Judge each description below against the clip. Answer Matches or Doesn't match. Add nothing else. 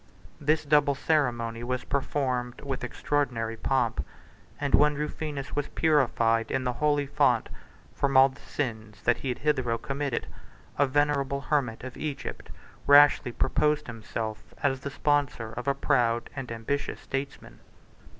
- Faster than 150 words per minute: Doesn't match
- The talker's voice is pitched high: Doesn't match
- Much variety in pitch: Doesn't match